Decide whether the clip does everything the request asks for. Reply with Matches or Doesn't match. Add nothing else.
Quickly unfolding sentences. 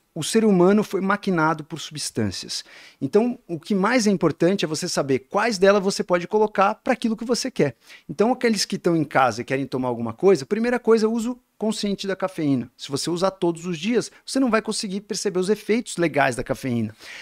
Matches